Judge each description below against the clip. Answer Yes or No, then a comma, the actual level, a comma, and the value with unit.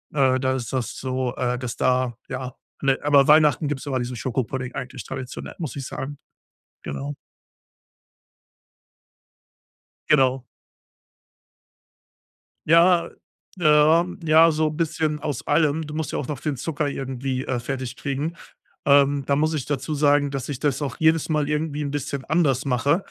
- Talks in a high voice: No, medium, 140 Hz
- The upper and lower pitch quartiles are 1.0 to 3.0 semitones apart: Yes, narrow, 2.6 semitones